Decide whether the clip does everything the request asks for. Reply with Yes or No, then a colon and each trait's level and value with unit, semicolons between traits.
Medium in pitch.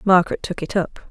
Yes: medium, 180 Hz